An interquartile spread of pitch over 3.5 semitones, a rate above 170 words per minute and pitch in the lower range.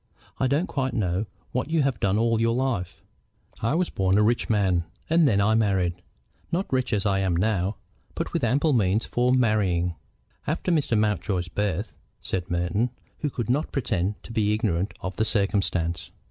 Yes: average, 4.8 semitones; average, 180 wpm; low, 105 Hz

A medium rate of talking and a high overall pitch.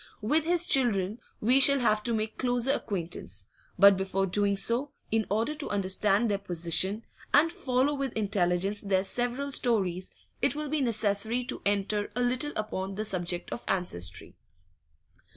Yes: average, 155 wpm; high, 215 Hz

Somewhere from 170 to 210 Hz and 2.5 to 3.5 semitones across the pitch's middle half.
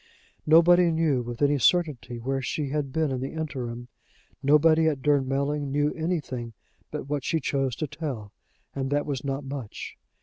No: medium, 140 Hz; average, 2.8 semitones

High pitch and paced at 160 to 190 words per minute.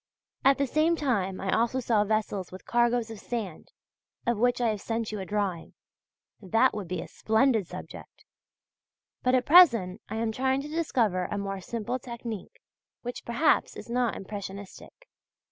Yes: high, 225 Hz; average, 165 wpm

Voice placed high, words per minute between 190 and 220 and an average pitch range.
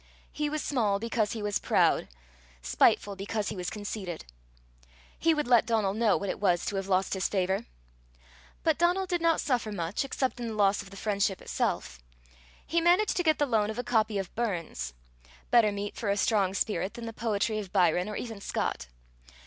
Yes: high, 210 Hz; average, 195 wpm; average, 3.6 semitones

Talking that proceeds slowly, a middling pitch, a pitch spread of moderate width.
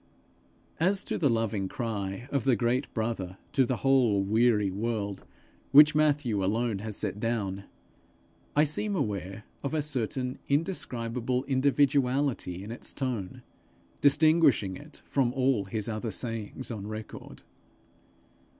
No: slow, 130 wpm; low, 120 Hz; average, 4.7 semitones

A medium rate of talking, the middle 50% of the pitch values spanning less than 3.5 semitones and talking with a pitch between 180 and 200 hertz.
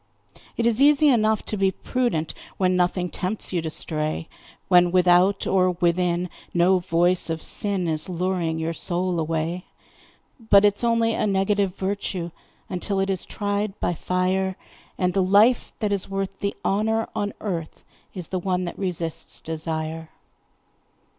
Yes: average, 155 wpm; average, 2.7 semitones; medium, 185 Hz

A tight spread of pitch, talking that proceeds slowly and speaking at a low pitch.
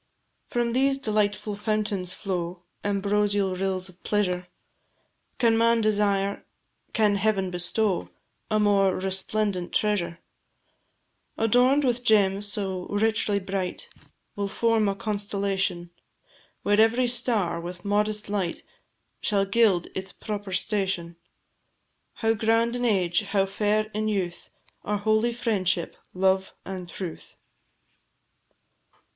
No: narrow, 2.3 semitones; slow, 110 wpm; high, 205 Hz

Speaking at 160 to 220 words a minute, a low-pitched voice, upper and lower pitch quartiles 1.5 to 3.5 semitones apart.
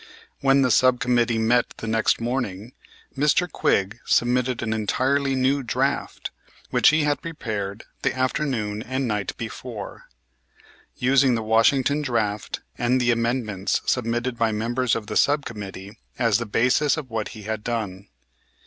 No: average, 150 wpm; low, 120 Hz; average, 3.0 semitones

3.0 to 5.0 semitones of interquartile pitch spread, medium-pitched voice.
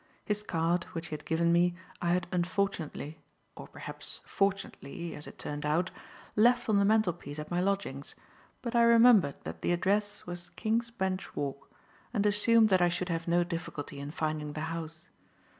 Yes: average, 4.0 semitones; medium, 175 Hz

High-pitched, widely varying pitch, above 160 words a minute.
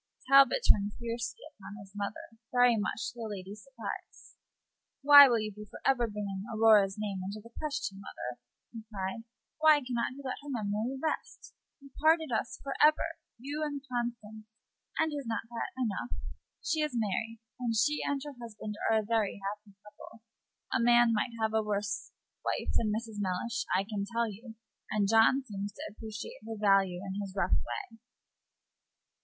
No: high, 225 Hz; average, 3.3 semitones; average, 175 wpm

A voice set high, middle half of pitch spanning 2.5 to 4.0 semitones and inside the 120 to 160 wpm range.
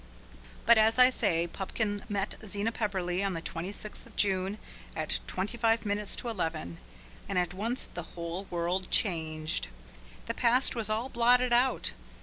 No: high, 205 Hz; average, 4.4 semitones; average, 155 wpm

